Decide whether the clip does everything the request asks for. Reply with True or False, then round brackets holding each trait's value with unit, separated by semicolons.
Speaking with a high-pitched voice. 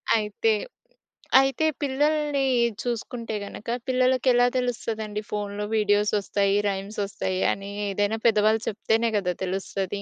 True (215 Hz)